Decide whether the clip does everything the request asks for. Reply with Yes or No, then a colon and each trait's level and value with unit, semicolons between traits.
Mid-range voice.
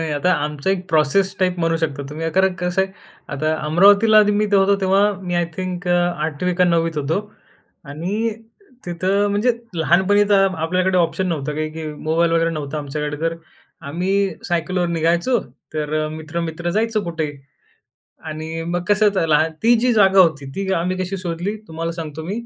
Yes: medium, 175 Hz